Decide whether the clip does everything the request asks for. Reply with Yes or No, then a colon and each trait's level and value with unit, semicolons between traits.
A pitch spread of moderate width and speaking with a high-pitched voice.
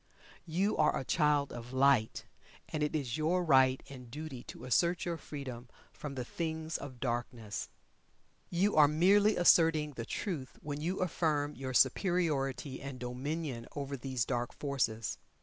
No: average, 3.8 semitones; medium, 145 Hz